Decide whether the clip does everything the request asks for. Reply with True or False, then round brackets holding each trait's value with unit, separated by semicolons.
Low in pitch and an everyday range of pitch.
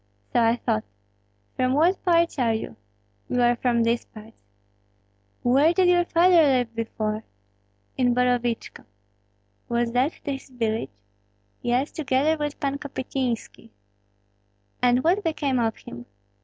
False (250 Hz; 4.1 semitones)